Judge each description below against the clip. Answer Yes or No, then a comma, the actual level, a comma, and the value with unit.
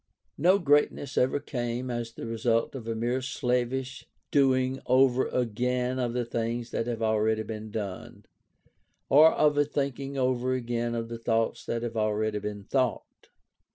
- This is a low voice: Yes, low, 120 Hz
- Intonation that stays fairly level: Yes, narrow, 2.3 semitones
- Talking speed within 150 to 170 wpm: Yes, average, 155 wpm